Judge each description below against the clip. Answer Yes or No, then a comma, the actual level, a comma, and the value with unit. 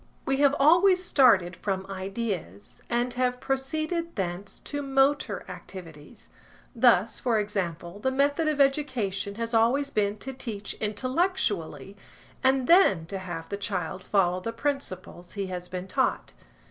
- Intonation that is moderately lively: No, wide, 6.4 semitones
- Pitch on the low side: No, high, 225 Hz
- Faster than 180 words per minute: No, average, 140 wpm